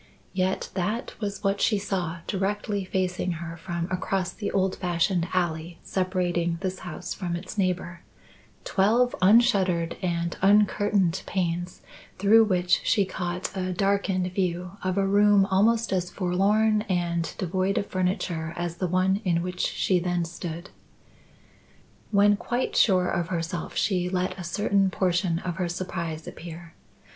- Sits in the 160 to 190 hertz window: Yes, medium, 185 Hz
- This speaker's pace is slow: No, average, 145 wpm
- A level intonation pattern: Yes, narrow, 2.2 semitones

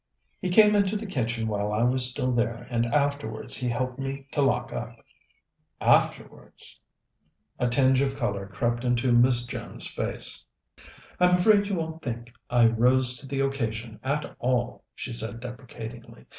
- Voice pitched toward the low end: Yes, low, 125 Hz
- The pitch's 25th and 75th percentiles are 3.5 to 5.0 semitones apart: No, average, 2.8 semitones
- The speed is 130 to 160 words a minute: Yes, average, 155 wpm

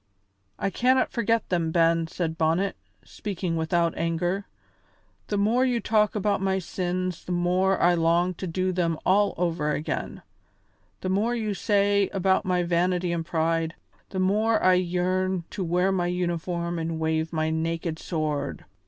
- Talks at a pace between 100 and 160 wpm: Yes, average, 155 wpm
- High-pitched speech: No, medium, 180 Hz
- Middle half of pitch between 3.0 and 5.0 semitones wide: No, narrow, 2.6 semitones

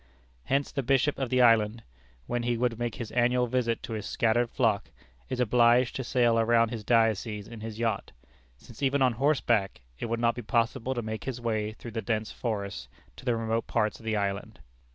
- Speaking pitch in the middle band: No, low, 115 Hz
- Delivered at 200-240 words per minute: Yes, fast, 205 wpm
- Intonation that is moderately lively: No, narrow, 2.0 semitones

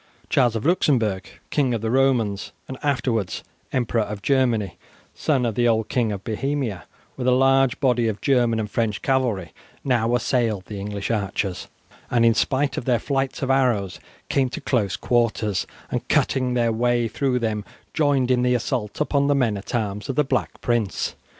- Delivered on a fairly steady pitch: No, average, 3.7 semitones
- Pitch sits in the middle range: No, low, 120 Hz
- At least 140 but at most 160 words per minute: No, average, 180 wpm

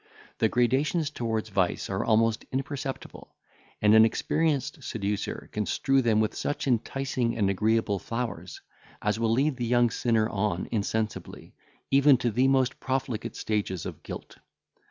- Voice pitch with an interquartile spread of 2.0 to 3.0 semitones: No, average, 3.7 semitones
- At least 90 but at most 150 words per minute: Yes, average, 145 wpm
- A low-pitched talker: Yes, low, 115 Hz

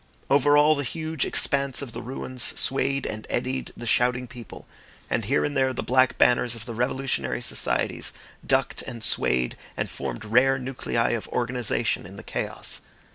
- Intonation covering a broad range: No, narrow, 2.5 semitones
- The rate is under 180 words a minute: Yes, average, 170 wpm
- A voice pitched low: Yes, low, 125 Hz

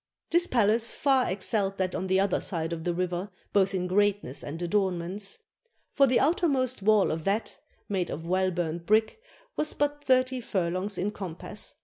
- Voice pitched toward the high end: Yes, high, 195 Hz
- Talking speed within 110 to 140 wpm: No, average, 175 wpm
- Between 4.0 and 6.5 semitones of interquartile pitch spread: Yes, average, 4.3 semitones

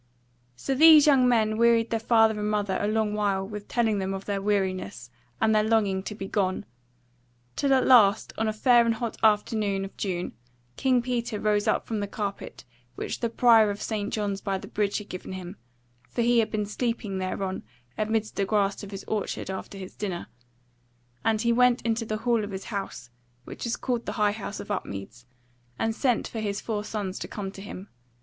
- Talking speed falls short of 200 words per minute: No, fast, 205 wpm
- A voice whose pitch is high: Yes, high, 210 Hz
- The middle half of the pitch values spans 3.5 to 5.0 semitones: No, narrow, 2.4 semitones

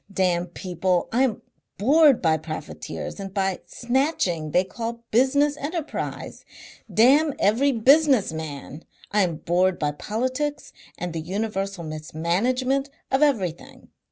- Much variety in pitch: Yes, wide, 7.4 semitones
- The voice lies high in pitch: Yes, high, 205 Hz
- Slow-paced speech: Yes, slow, 130 wpm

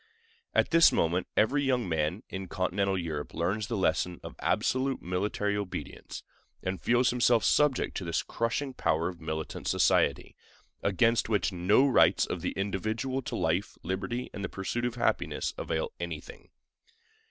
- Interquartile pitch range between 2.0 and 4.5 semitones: No, average, 5.1 semitones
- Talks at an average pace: Yes, average, 155 wpm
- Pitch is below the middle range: Yes, low, 100 Hz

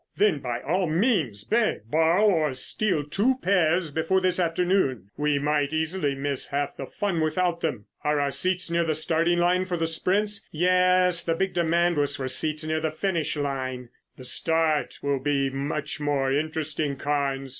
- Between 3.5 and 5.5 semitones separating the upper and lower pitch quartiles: Yes, average, 4.0 semitones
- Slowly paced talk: No, average, 175 wpm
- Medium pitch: Yes, medium, 160 Hz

